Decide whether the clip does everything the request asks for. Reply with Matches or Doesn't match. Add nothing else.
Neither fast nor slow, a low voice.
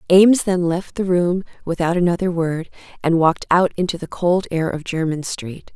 Doesn't match